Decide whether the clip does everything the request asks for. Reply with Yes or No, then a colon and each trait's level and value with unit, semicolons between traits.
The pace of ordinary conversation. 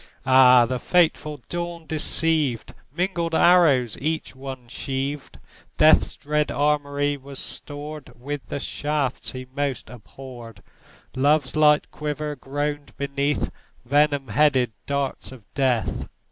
No: slow, 115 wpm